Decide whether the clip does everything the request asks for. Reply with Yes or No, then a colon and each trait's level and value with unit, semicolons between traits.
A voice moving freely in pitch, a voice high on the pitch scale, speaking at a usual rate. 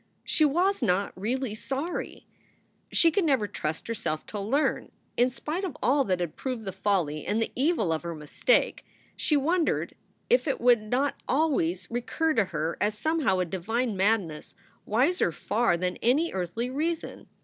Yes: wide, 7.7 semitones; high, 230 Hz; average, 165 wpm